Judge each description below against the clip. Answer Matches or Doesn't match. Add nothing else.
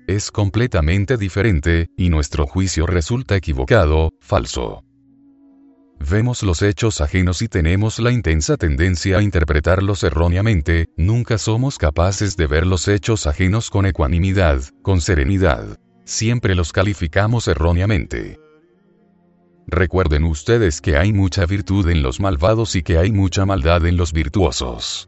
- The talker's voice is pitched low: Matches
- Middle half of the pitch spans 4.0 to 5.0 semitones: Matches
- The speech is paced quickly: Doesn't match